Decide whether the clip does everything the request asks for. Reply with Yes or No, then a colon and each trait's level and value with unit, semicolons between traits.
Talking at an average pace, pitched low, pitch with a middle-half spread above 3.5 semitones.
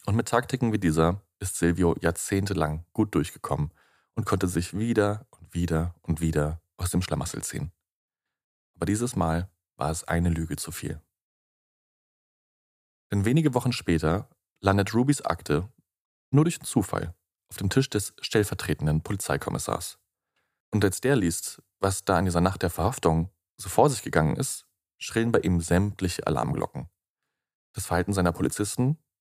Yes: average, 150 wpm; very low, 95 Hz; average, 3.9 semitones